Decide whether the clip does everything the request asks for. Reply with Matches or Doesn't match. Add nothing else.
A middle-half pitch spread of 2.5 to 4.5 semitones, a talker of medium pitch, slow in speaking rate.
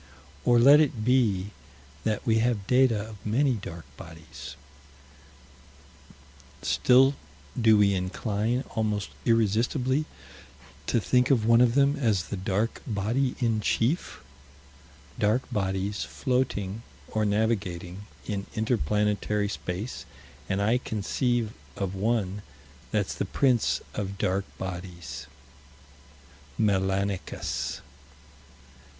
Doesn't match